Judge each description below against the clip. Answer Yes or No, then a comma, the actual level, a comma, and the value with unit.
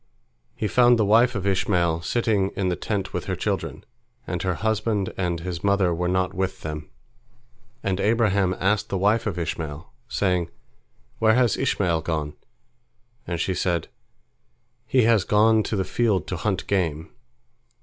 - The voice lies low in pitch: Yes, very low, 95 Hz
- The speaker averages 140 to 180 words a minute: Yes, average, 160 wpm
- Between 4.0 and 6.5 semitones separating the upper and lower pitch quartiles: No, average, 3.4 semitones